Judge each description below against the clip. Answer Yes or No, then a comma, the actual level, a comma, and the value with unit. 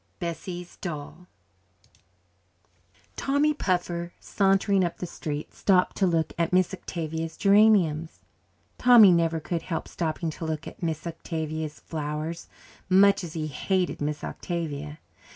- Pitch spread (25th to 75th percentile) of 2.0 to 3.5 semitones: Yes, average, 2.8 semitones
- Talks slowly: Yes, slow, 125 wpm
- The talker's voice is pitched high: No, medium, 170 Hz